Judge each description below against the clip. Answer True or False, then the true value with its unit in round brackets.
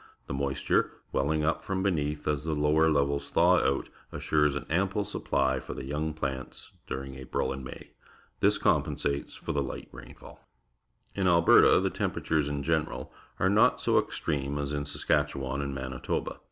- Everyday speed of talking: True (165 wpm)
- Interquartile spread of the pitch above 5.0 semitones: False (2.5 semitones)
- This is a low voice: True (70 Hz)